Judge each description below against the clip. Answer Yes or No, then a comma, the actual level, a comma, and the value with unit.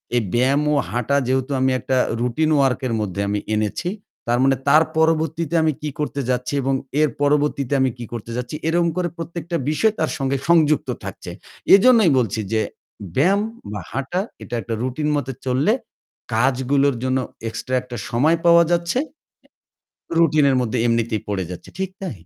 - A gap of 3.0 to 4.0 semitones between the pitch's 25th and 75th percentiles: No, average, 4.4 semitones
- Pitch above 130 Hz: Yes, medium, 140 Hz